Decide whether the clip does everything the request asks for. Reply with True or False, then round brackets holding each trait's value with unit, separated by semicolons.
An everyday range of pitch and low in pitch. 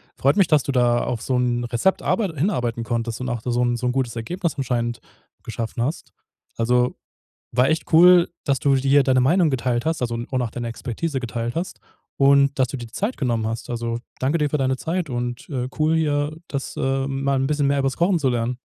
True (3.4 semitones; 130 Hz)